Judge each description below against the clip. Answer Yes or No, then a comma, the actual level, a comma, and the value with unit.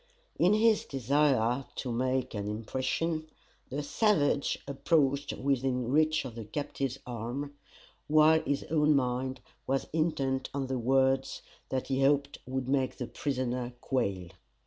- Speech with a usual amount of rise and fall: No, narrow, 2.3 semitones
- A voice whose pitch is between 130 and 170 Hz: Yes, low, 135 Hz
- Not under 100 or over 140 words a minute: Yes, slow, 135 wpm